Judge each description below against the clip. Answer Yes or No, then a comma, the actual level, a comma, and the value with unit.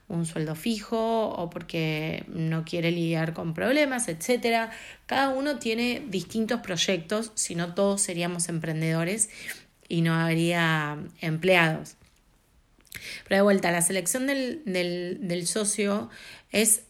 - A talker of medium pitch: Yes, medium, 180 Hz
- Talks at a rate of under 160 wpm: Yes, slow, 125 wpm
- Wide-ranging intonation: No, average, 4.9 semitones